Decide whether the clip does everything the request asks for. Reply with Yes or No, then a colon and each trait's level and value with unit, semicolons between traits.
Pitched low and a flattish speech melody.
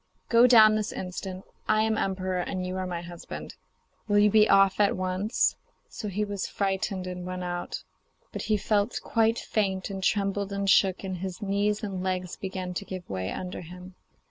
No: high, 195 Hz; narrow, 2.1 semitones